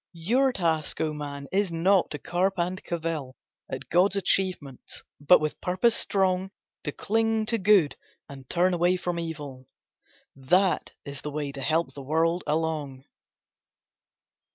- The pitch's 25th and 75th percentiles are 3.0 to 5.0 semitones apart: Yes, average, 4.2 semitones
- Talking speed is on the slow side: No, average, 145 wpm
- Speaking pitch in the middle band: Yes, medium, 165 Hz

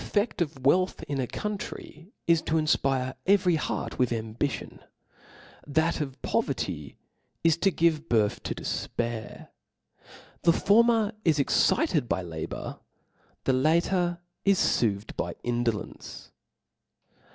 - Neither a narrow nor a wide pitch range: No, wide, 6.4 semitones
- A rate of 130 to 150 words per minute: Yes, average, 145 wpm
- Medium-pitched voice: Yes, medium, 150 Hz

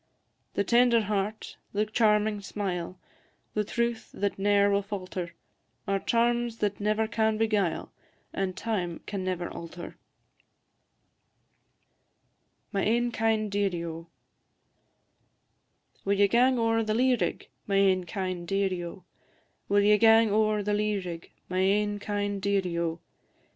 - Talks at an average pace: No, slow, 130 wpm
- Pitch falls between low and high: No, high, 205 Hz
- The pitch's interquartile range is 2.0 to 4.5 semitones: Yes, narrow, 2.5 semitones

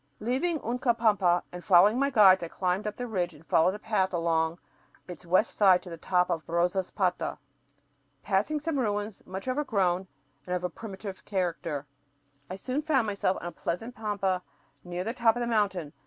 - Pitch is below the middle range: No, high, 195 Hz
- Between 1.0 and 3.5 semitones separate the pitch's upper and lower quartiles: No, average, 4.1 semitones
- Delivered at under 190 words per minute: Yes, average, 180 wpm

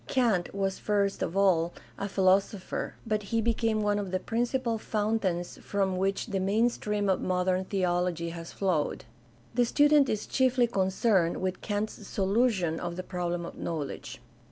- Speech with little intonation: No, average, 3.2 semitones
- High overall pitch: Yes, high, 195 Hz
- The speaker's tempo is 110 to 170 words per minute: Yes, average, 155 wpm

